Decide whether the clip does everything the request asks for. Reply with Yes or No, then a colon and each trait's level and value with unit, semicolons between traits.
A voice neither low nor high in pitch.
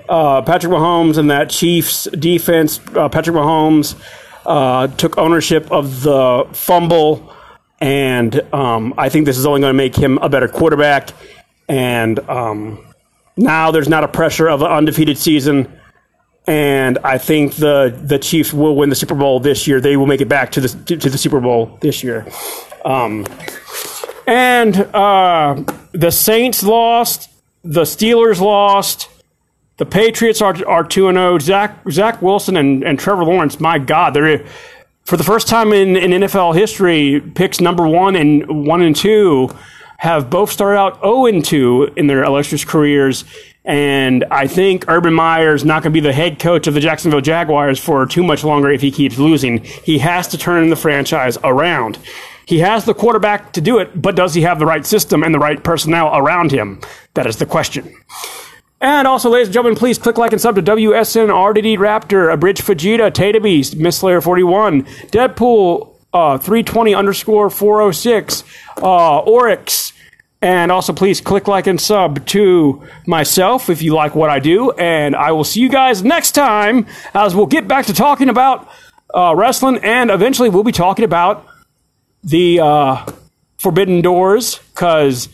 Yes: medium, 170 Hz